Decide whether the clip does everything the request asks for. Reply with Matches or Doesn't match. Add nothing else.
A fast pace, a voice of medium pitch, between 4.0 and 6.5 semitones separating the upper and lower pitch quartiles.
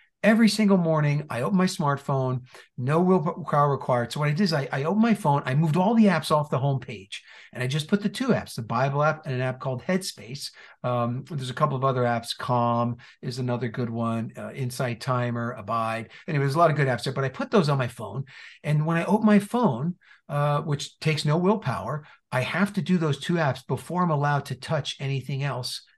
Matches